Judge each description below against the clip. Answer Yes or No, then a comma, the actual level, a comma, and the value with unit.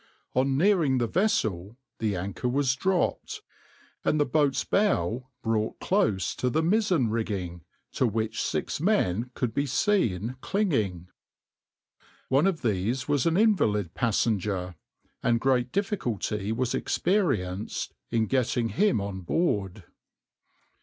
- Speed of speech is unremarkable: No, slow, 125 wpm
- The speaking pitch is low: Yes, low, 125 Hz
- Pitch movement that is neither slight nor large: No, wide, 7.3 semitones